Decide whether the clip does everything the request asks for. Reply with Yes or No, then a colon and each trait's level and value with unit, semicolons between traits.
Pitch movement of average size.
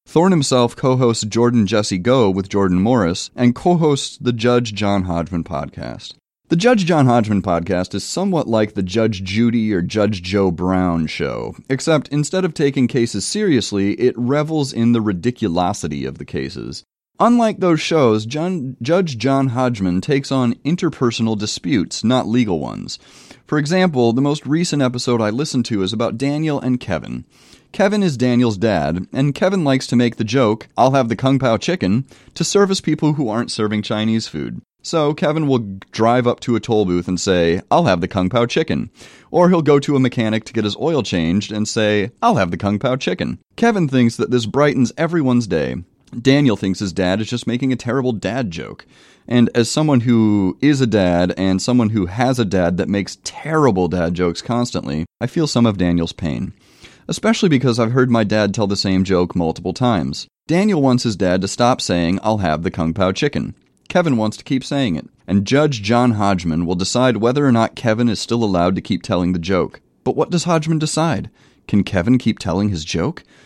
No: wide, 5.8 semitones